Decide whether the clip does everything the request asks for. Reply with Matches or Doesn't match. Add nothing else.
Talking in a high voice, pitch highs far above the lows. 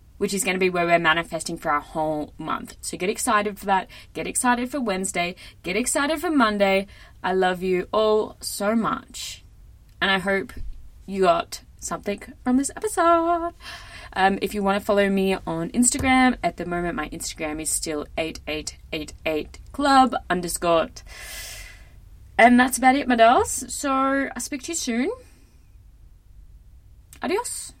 Matches